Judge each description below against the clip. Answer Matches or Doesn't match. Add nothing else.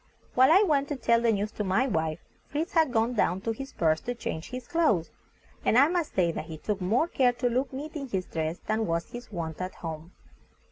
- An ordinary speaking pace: Doesn't match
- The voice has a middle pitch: Doesn't match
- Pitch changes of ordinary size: Doesn't match